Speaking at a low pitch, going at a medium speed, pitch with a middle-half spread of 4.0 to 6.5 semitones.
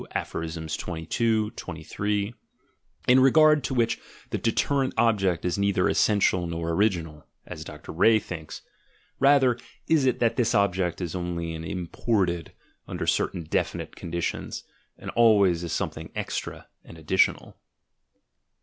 No: very low, 95 Hz; slow, 125 wpm; wide, 5.4 semitones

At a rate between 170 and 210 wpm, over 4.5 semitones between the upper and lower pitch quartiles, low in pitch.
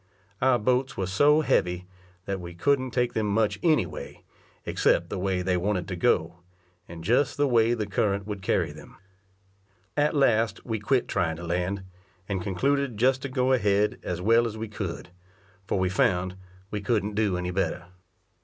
Yes: average, 180 wpm; average, 5.2 semitones; low, 105 Hz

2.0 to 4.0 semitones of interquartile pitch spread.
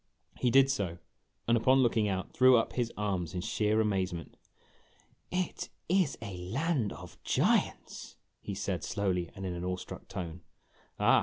No: wide, 5.6 semitones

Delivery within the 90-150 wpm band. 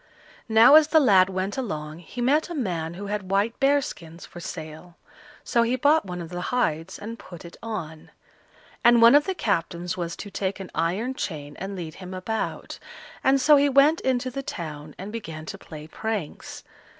No: average, 195 wpm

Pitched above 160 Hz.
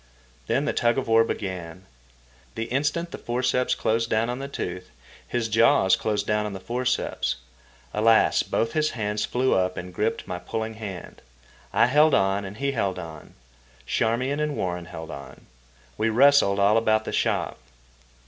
No: low, 110 Hz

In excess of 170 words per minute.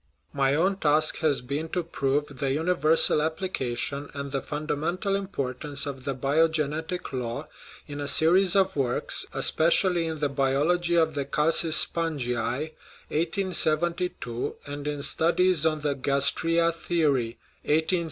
No: slow, 135 wpm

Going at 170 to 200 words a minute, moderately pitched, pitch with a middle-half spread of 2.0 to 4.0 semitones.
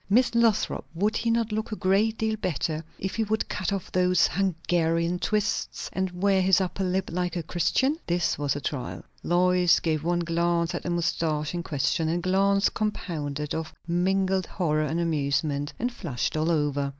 Yes: average, 180 wpm; medium, 175 Hz; average, 3.3 semitones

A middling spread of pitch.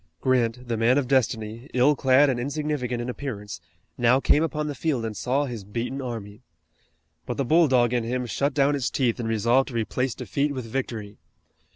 Yes: average, 3.1 semitones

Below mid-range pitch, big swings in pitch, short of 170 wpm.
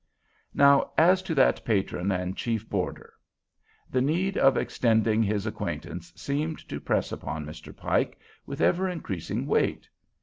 Yes: low, 115 Hz; wide, 7.9 semitones; average, 140 wpm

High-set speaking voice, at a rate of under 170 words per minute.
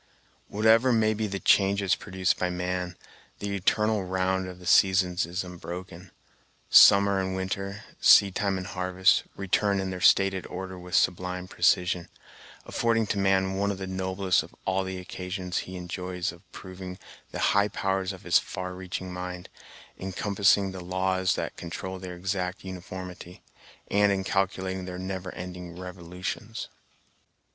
No: very low, 95 Hz; average, 155 wpm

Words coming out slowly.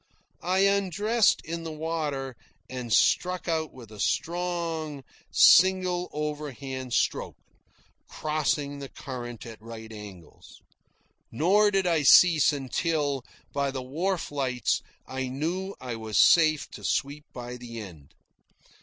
Yes: slow, 125 wpm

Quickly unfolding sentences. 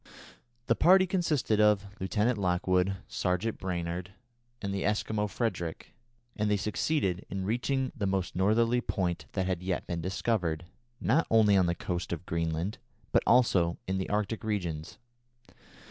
No: average, 145 wpm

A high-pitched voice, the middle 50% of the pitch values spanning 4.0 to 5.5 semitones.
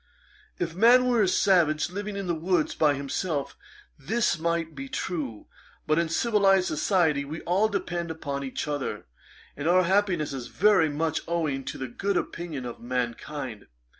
No: medium, 165 Hz; average, 4.7 semitones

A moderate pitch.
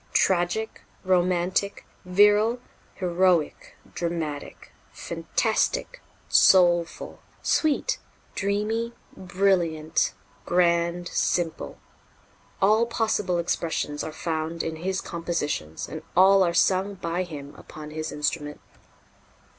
Yes: medium, 175 Hz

